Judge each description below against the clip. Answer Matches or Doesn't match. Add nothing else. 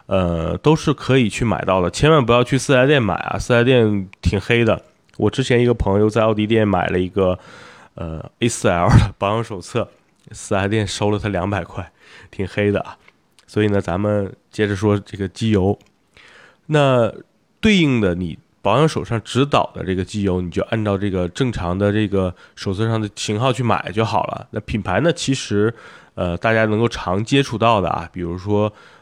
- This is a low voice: Matches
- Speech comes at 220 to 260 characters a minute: Doesn't match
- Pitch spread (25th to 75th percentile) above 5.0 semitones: Doesn't match